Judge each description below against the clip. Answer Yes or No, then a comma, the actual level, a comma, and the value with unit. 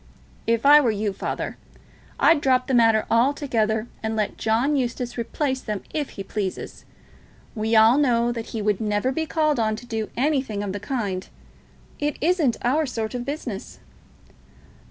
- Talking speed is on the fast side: No, average, 165 wpm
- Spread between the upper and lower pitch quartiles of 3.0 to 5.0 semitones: Yes, average, 4.1 semitones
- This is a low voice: No, high, 235 Hz